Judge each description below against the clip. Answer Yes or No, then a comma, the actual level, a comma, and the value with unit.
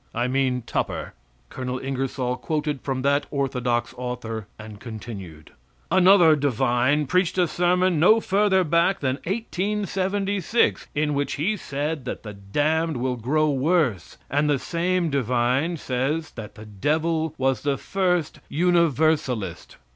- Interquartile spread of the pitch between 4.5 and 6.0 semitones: Yes, average, 5.2 semitones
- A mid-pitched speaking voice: Yes, medium, 145 Hz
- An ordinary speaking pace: No, slow, 130 wpm